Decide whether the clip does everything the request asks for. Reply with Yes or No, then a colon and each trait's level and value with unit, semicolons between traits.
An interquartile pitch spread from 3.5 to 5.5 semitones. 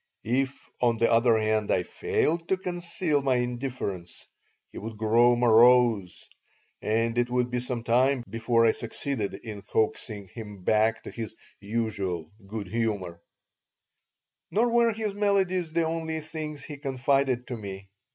Yes: average, 4.5 semitones